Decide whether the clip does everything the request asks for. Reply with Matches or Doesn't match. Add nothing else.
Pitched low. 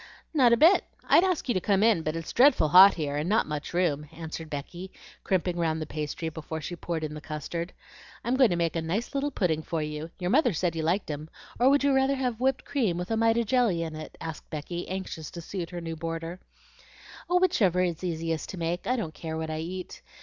Doesn't match